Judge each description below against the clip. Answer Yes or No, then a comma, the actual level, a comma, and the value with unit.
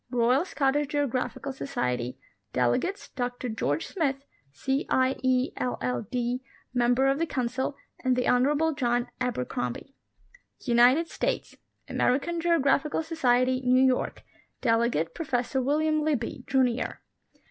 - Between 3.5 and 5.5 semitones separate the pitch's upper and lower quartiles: No, average, 2.8 semitones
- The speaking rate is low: Yes, slow, 120 wpm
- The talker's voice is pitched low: No, very high, 255 Hz